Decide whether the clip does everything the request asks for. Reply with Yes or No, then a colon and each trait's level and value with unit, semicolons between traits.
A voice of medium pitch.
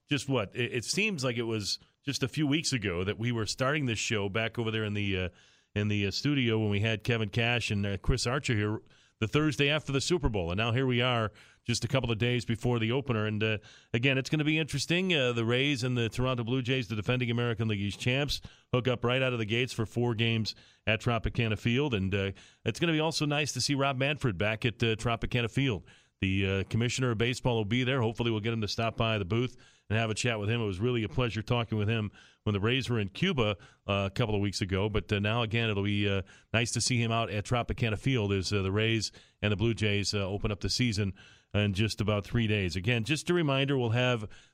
No: low, 115 Hz